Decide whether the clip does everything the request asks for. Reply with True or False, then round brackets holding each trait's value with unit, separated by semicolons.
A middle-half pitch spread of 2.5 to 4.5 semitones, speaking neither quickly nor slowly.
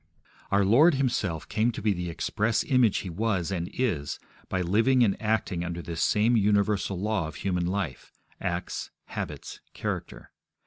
True (4.1 semitones; 160 wpm)